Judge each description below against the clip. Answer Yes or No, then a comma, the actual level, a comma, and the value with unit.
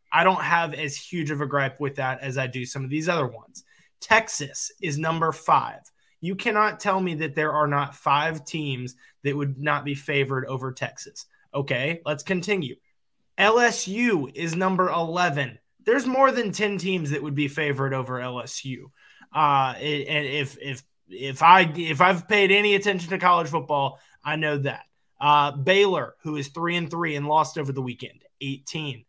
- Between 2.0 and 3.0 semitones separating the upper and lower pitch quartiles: No, average, 4.3 semitones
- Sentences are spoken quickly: No, average, 180 wpm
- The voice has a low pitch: No, medium, 150 Hz